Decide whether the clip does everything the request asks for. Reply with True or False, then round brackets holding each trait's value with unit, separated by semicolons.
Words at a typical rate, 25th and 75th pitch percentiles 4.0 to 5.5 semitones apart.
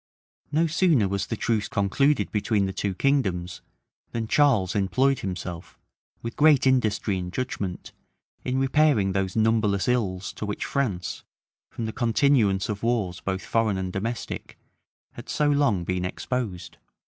True (145 wpm; 5.1 semitones)